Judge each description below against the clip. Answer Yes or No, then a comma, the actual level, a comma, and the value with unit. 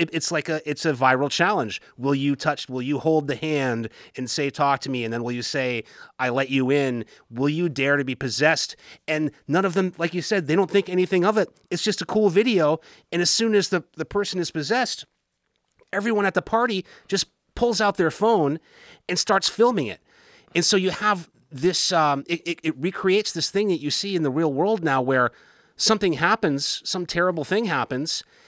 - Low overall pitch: No, medium, 170 Hz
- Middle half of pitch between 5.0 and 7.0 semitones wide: Yes, wide, 5.5 semitones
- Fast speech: Yes, fast, 215 wpm